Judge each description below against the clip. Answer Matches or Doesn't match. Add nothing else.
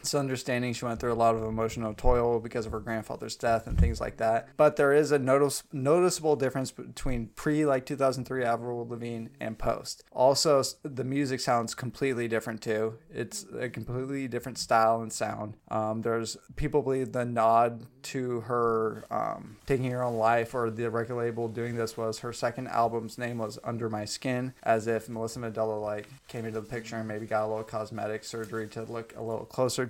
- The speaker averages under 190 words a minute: Doesn't match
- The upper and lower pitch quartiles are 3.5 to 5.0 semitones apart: Doesn't match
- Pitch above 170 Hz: Doesn't match